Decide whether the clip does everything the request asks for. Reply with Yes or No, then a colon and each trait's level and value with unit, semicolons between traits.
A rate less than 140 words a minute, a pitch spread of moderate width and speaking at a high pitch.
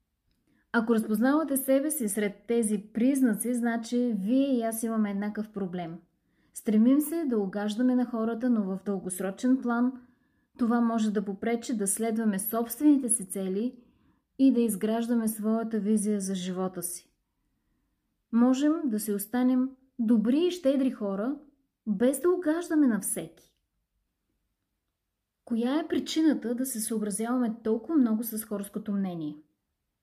Yes: average, 130 wpm; average, 3.7 semitones; high, 230 Hz